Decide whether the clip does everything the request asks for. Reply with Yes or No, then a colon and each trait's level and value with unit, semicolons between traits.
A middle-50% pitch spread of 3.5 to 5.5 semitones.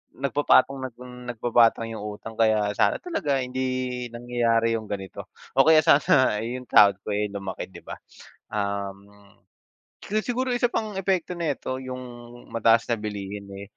Yes: average, 4.4 semitones